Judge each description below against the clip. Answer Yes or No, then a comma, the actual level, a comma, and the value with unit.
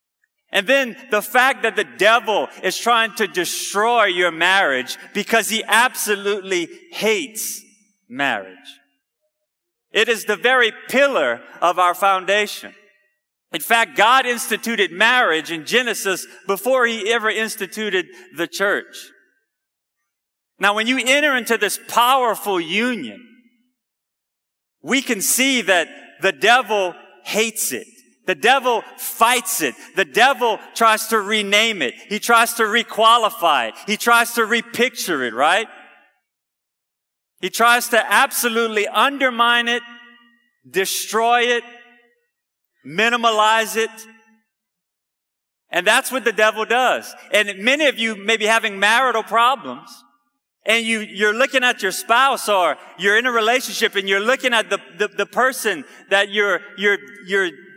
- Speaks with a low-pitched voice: No, high, 225 Hz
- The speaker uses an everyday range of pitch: Yes, average, 3.4 semitones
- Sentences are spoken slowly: Yes, slow, 130 wpm